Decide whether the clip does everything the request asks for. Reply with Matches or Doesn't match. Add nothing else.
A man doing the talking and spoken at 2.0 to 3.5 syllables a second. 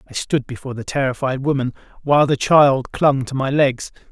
Doesn't match